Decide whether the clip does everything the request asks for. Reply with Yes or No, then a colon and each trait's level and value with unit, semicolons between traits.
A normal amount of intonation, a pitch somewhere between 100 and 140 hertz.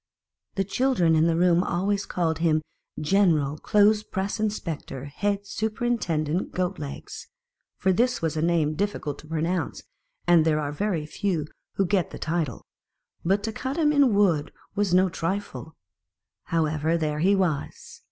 No: average, 4.4 semitones; medium, 175 Hz